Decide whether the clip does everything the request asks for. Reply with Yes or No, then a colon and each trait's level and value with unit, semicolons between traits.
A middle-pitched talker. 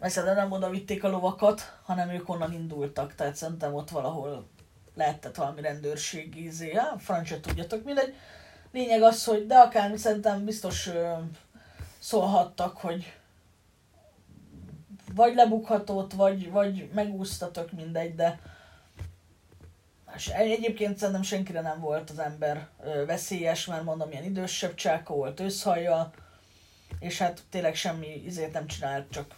Yes: medium, 170 Hz